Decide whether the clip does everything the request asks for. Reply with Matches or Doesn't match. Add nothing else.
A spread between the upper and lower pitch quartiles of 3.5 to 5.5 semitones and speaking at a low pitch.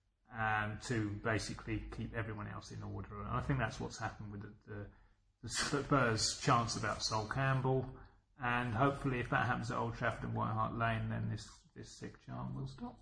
Doesn't match